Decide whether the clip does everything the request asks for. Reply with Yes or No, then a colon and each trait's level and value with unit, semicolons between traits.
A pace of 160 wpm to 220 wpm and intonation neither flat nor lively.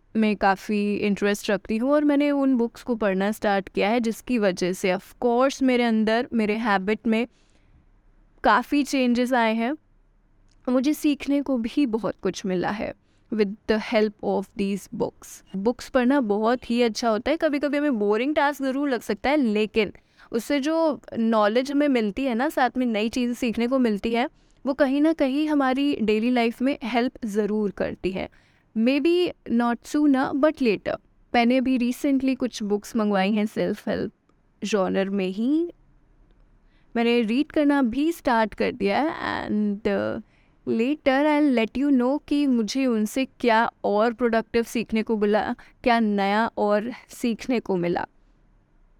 Yes: average, 165 wpm; average, 4.0 semitones